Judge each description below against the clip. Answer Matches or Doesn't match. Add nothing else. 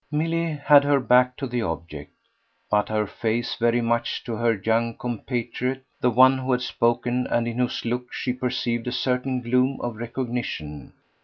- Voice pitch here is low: Matches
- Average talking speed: Matches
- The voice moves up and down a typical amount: Doesn't match